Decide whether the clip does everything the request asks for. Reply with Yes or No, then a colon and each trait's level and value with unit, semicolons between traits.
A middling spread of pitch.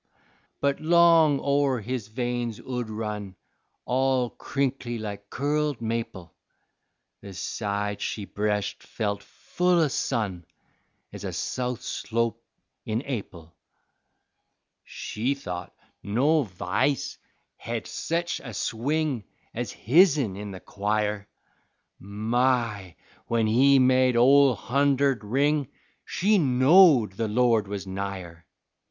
Yes: average, 5.0 semitones